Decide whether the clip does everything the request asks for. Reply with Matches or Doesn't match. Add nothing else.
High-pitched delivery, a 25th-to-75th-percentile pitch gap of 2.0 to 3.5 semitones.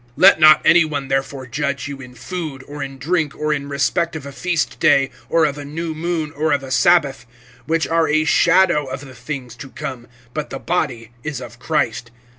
Doesn't match